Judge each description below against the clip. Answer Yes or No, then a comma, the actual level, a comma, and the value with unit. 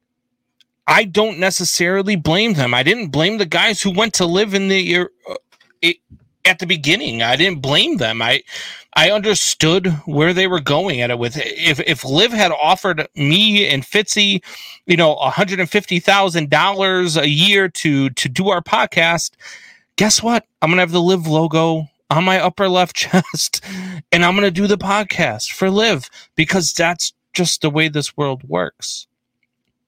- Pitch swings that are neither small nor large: Yes, average, 4.0 semitones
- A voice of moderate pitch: Yes, medium, 180 Hz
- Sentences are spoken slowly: No, average, 175 wpm